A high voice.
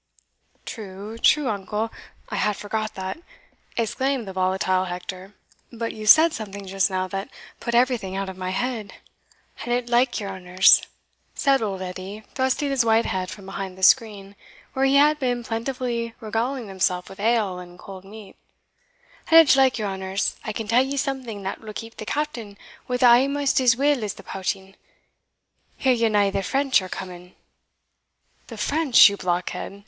Yes: high, 215 Hz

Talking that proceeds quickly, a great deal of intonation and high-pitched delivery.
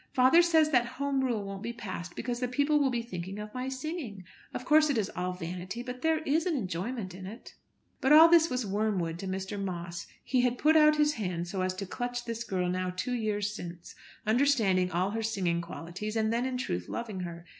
Yes: fast, 220 wpm; wide, 5.7 semitones; high, 220 Hz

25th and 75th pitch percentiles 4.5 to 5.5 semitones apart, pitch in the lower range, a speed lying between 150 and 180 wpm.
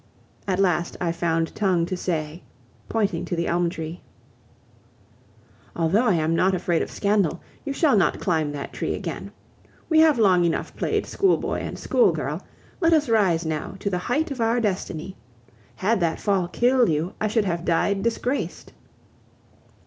No: average, 5.0 semitones; medium, 185 Hz; average, 165 wpm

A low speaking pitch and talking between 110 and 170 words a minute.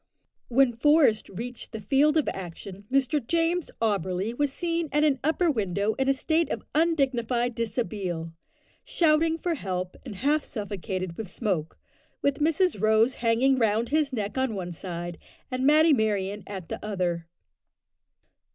No: high, 235 Hz; average, 150 wpm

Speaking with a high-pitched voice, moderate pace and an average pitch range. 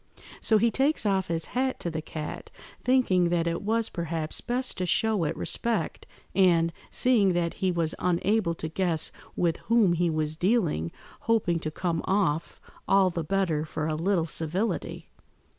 No: medium, 175 Hz; average, 165 wpm; average, 4.1 semitones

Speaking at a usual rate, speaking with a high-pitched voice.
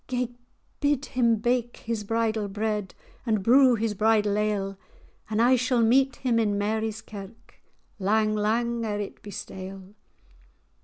Yes: average, 145 wpm; high, 220 Hz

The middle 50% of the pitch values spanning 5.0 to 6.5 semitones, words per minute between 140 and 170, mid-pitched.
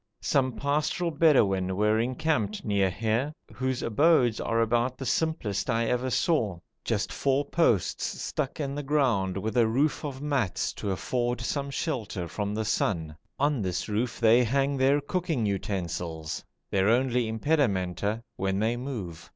No: wide, 5.4 semitones; average, 150 wpm; low, 120 Hz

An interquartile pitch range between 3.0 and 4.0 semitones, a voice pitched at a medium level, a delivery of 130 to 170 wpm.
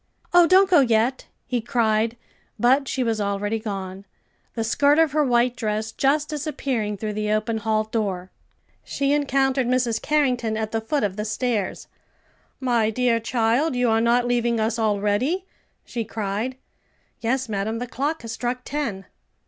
No: average, 3.3 semitones; high, 235 Hz; average, 160 wpm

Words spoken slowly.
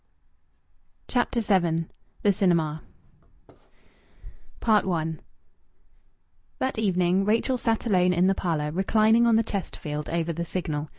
Yes: slow, 110 wpm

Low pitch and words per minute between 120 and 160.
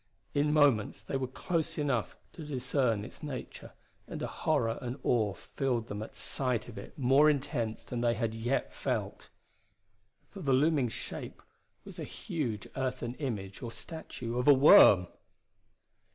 Yes: low, 125 Hz; average, 155 wpm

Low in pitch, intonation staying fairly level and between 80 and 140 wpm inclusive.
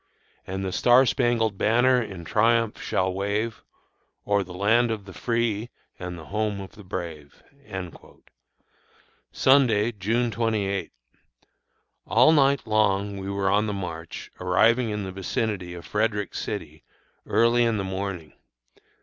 No: low, 105 Hz; average, 3.2 semitones; slow, 135 wpm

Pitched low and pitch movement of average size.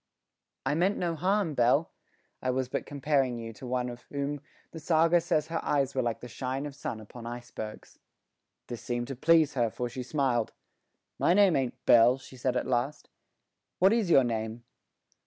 Yes: low, 130 Hz; average, 4.3 semitones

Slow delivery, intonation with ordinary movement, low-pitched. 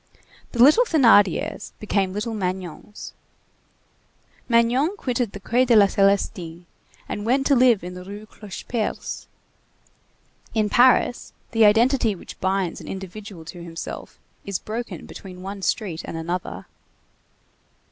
No: slow, 125 wpm; average, 4.2 semitones; high, 205 Hz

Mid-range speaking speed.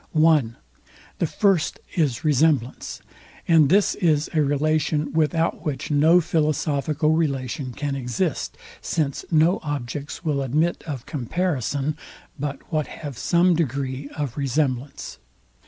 No: slow, 120 wpm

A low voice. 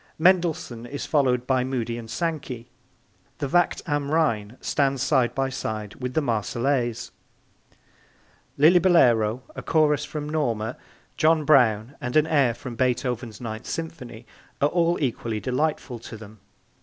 Yes: low, 130 Hz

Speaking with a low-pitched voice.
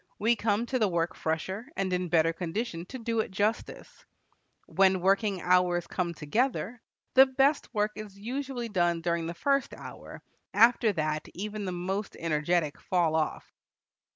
No: high, 190 Hz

